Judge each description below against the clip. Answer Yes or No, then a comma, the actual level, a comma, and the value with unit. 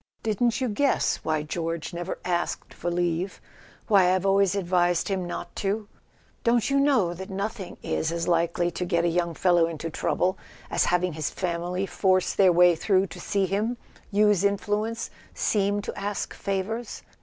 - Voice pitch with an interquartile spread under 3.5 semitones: Yes, average, 2.8 semitones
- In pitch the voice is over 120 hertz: Yes, medium, 185 Hz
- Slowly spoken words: No, average, 165 wpm